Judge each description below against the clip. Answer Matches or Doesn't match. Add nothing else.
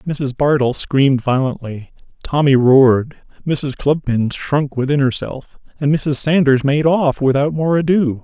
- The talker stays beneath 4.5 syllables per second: Matches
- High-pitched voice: Doesn't match